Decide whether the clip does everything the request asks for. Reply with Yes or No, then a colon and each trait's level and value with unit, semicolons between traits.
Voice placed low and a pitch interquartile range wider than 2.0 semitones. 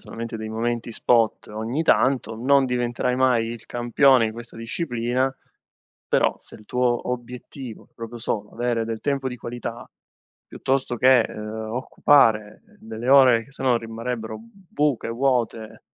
Yes: low, 120 Hz; narrow, 2.4 semitones